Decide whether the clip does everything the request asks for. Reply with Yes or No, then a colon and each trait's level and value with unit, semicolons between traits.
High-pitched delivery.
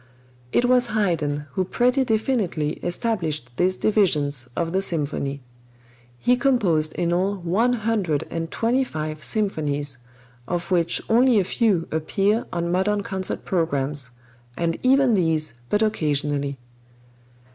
No: medium, 175 Hz